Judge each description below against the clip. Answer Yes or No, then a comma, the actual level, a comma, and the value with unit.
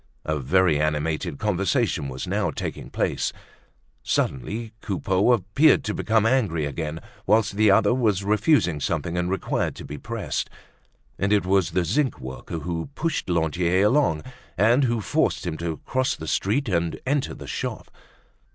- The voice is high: No, very low, 95 Hz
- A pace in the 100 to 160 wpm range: Yes, average, 155 wpm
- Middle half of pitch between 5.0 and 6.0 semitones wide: Yes, average, 5.3 semitones